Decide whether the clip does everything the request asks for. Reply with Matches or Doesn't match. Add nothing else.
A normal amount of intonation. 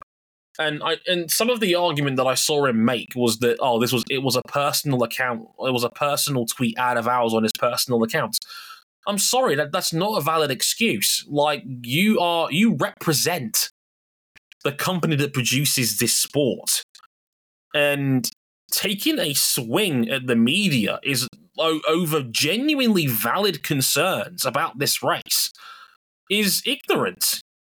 Doesn't match